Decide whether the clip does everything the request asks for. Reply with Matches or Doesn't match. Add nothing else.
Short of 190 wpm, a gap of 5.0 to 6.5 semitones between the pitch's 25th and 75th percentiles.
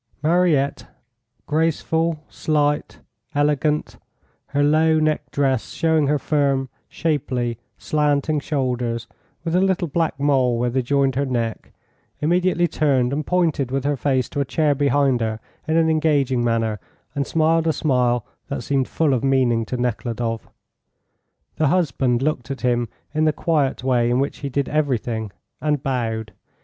Doesn't match